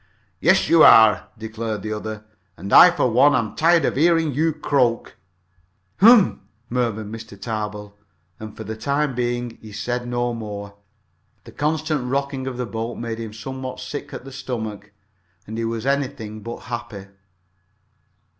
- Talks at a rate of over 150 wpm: Yes, average, 160 wpm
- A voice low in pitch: Yes, low, 120 Hz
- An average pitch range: Yes, average, 3.9 semitones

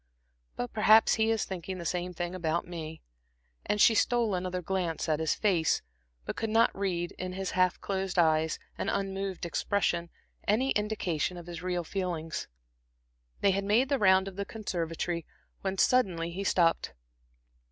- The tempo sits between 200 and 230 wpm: No, average, 165 wpm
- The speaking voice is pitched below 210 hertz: Yes, medium, 185 Hz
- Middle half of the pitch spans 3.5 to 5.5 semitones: No, average, 2.8 semitones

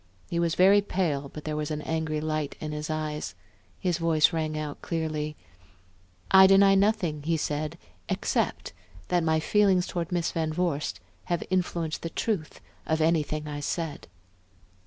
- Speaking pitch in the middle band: Yes, medium, 160 Hz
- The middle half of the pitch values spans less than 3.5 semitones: Yes, narrow, 2.5 semitones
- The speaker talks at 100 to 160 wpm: Yes, average, 155 wpm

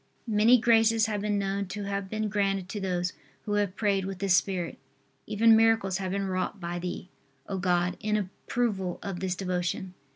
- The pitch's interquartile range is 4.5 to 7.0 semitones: No, narrow, 2.4 semitones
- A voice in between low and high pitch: No, high, 195 Hz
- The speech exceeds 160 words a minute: Yes, average, 185 wpm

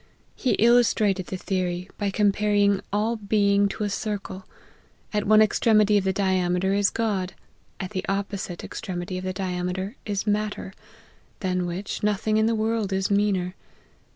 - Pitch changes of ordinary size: No, narrow, 2.0 semitones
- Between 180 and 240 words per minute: No, average, 160 wpm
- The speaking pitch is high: Yes, high, 200 Hz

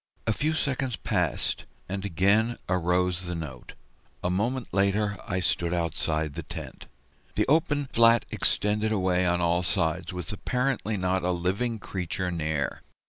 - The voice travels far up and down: No, average, 4.0 semitones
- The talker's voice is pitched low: Yes, very low, 95 Hz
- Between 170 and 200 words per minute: No, average, 145 wpm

